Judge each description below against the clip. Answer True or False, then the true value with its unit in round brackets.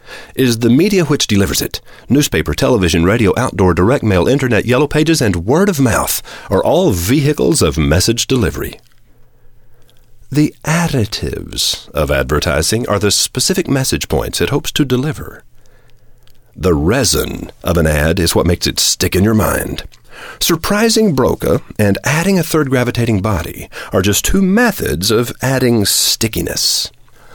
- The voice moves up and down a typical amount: False (6.4 semitones)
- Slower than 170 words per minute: True (145 wpm)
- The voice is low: True (120 Hz)